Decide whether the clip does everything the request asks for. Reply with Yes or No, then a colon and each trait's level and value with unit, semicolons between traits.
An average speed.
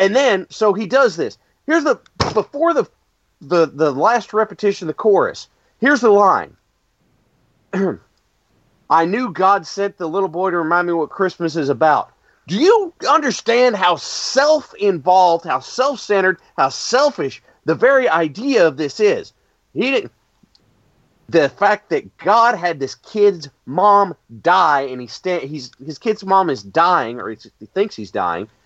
Yes: average, 160 wpm